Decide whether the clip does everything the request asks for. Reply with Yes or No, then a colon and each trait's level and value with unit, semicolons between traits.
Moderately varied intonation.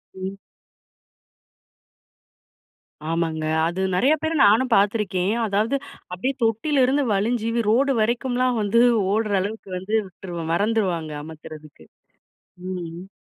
Yes: average, 5.0 semitones